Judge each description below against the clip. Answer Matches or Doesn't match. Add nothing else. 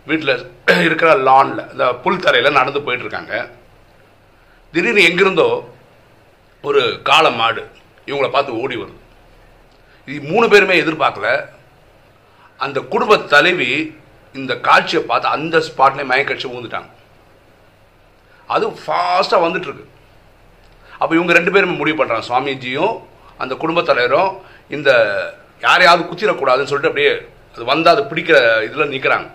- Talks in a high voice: Doesn't match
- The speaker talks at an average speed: Matches